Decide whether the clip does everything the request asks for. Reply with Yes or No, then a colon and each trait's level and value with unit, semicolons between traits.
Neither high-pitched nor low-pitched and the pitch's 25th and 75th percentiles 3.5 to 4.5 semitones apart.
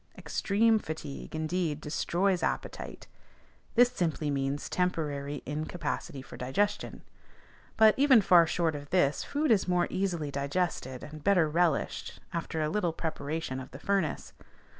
Yes: medium, 165 Hz; average, 4.2 semitones